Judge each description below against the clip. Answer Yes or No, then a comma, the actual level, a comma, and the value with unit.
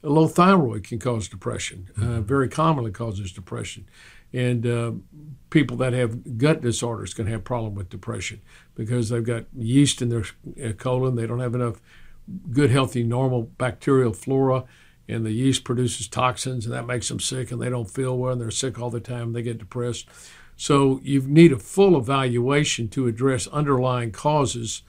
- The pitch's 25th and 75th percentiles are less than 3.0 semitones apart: Yes, narrow, 2.6 semitones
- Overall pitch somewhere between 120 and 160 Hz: Yes, low, 125 Hz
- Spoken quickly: No, average, 180 wpm